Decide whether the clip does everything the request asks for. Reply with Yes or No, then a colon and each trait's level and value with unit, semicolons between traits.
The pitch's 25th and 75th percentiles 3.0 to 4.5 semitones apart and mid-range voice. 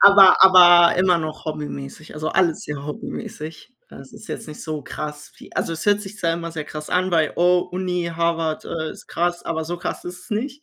No: narrow, 2.6 semitones; medium, 170 Hz